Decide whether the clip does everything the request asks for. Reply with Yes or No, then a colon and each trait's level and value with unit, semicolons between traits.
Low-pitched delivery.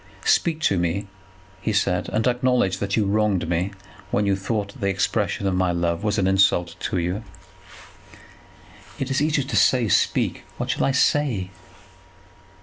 Yes: low, 100 Hz